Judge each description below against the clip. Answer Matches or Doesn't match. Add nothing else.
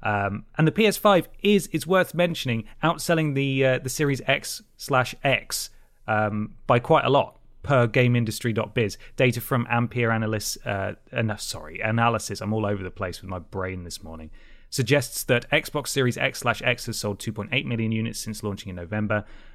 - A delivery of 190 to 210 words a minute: Doesn't match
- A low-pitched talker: Matches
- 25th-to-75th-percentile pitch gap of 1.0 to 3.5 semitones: Doesn't match